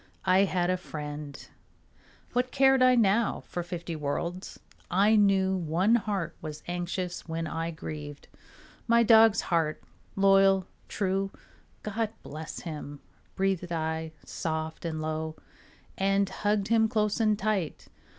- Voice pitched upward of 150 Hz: Yes, medium, 185 Hz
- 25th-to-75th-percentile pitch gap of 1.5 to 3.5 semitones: No, average, 4.3 semitones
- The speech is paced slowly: Yes, slow, 130 wpm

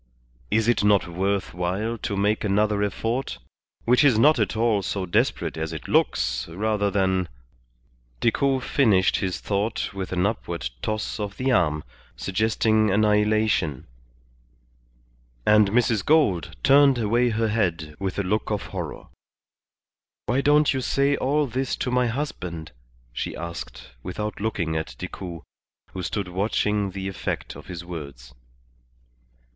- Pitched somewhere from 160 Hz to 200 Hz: No, low, 105 Hz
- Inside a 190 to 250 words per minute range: No, average, 140 wpm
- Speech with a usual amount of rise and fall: Yes, average, 4.0 semitones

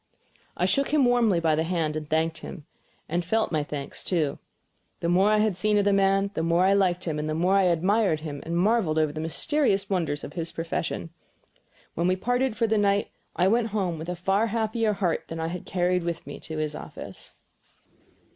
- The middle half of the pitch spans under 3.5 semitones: No, average, 4.2 semitones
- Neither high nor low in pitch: Yes, medium, 180 Hz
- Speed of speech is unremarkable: No, fast, 220 wpm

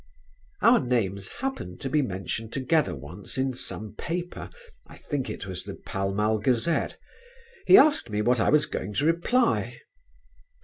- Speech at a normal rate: Yes, average, 160 wpm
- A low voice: Yes, low, 125 Hz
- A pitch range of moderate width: No, wide, 7.7 semitones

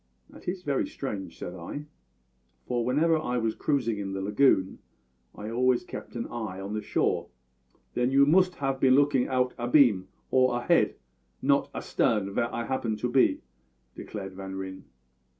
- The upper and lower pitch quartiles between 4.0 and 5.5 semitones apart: Yes, average, 4.7 semitones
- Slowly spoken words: No, average, 165 wpm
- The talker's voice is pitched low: Yes, low, 120 Hz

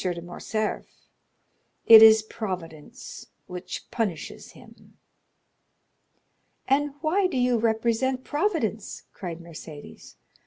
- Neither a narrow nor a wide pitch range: No, wide, 6.4 semitones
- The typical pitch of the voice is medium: No, high, 220 Hz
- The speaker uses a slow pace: Yes, slow, 90 wpm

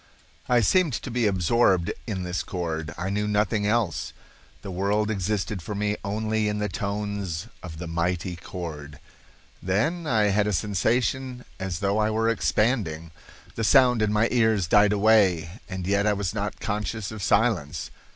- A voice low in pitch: Yes, low, 105 Hz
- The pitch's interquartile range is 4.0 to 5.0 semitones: No, average, 3.2 semitones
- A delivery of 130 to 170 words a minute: Yes, average, 165 wpm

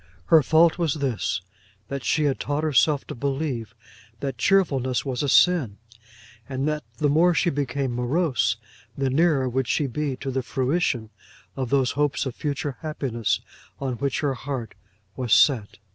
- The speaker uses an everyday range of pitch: Yes, average, 3.1 semitones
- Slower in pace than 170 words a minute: Yes, average, 160 wpm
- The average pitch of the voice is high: No, low, 135 Hz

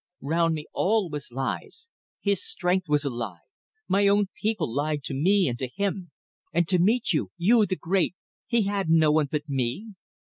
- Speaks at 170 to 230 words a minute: Yes, average, 185 wpm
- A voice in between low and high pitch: Yes, medium, 170 Hz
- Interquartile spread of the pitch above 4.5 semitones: Yes, average, 5.3 semitones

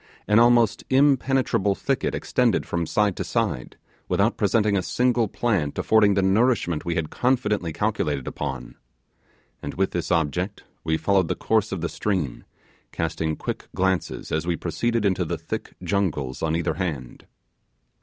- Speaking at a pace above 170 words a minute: No, average, 155 wpm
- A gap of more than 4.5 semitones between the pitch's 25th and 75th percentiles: Yes, average, 5.2 semitones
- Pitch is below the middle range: Yes, very low, 95 Hz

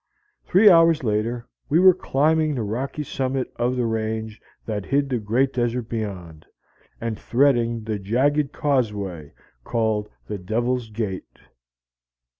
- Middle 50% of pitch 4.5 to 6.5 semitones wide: No, average, 4.1 semitones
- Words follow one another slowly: Yes, slow, 130 wpm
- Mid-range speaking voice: No, low, 120 Hz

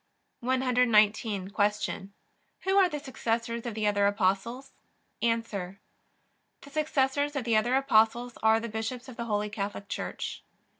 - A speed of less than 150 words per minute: Yes, average, 140 wpm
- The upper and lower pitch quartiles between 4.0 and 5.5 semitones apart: No, average, 3.5 semitones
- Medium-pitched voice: No, high, 230 Hz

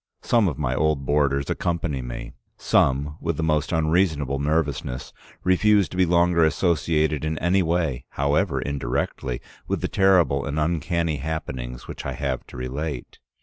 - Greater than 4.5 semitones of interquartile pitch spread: No, average, 3.5 semitones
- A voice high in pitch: No, very low, 75 Hz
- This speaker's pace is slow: No, average, 150 wpm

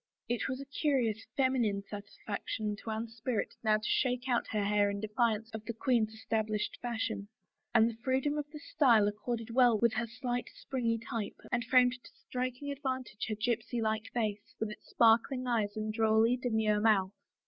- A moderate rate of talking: Yes, average, 180 wpm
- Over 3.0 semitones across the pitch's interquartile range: No, narrow, 2.6 semitones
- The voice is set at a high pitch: Yes, high, 230 Hz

